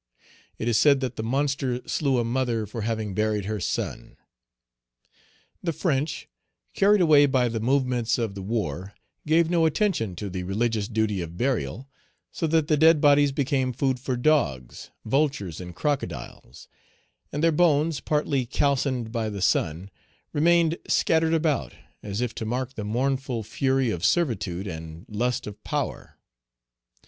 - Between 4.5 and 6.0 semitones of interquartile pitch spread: Yes, wide, 5.4 semitones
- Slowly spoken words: No, average, 155 wpm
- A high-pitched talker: No, low, 125 Hz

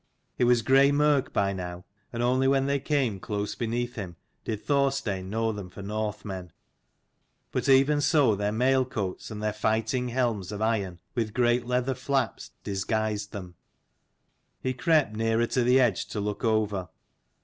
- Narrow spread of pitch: No, average, 4.0 semitones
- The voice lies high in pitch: No, low, 115 Hz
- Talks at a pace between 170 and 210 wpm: No, average, 160 wpm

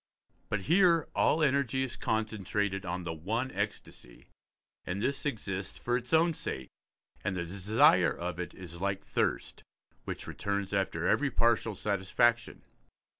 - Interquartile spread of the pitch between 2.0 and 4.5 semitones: No, average, 5.1 semitones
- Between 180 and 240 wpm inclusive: No, average, 140 wpm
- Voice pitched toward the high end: No, low, 100 Hz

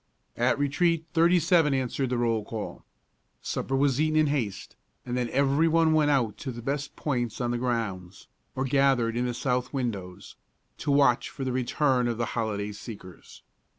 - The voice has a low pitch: Yes, low, 125 Hz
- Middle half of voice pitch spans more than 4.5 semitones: No, average, 3.5 semitones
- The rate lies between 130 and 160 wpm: No, average, 180 wpm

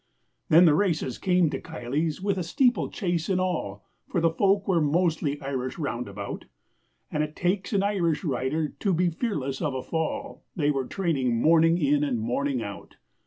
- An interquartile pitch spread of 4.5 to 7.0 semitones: Yes, average, 4.9 semitones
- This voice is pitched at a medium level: Yes, medium, 160 Hz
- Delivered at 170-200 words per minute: Yes, average, 175 wpm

